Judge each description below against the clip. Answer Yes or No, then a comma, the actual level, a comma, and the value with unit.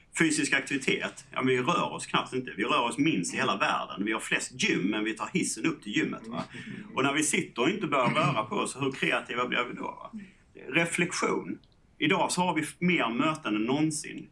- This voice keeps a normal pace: No, fast, 220 wpm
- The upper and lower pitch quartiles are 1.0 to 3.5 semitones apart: No, wide, 5.5 semitones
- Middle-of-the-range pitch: Yes, medium, 155 Hz